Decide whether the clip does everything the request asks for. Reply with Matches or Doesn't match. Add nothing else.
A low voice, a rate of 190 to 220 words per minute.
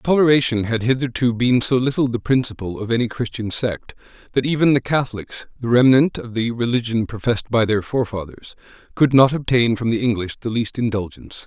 Doesn't match